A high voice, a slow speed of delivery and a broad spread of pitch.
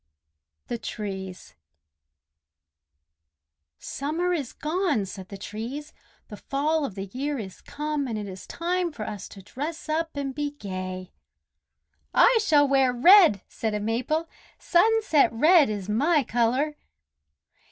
Yes: very high, 275 Hz; slow, 130 wpm; wide, 6.7 semitones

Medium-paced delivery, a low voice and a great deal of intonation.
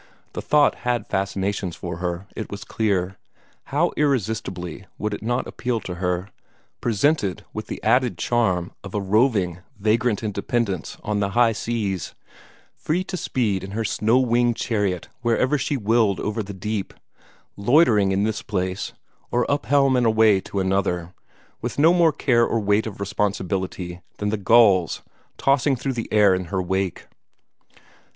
No: average, 160 wpm; low, 105 Hz; average, 3.9 semitones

